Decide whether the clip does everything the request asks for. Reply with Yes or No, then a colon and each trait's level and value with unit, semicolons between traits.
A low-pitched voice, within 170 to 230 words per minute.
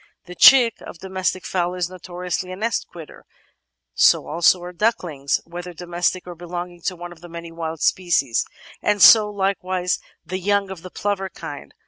No: medium, 180 Hz; average, 175 wpm